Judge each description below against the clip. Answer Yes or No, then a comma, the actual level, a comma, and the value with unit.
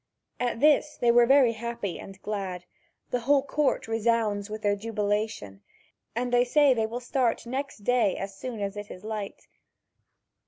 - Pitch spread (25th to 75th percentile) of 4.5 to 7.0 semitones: No, average, 3.3 semitones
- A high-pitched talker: Yes, high, 230 Hz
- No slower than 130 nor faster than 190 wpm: Yes, average, 165 wpm